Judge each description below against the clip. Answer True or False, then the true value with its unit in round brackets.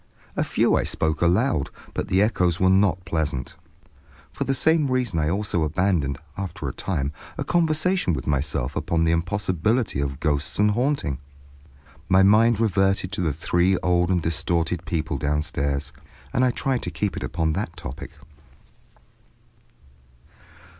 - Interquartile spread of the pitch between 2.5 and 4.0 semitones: False (5.0 semitones)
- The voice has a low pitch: True (90 Hz)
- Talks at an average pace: True (150 wpm)